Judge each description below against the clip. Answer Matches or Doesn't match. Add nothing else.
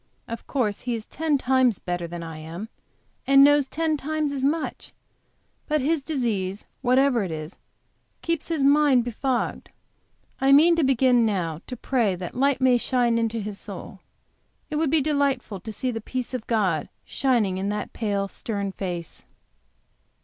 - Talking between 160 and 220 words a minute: Matches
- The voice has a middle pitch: Doesn't match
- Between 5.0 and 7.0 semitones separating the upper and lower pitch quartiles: Matches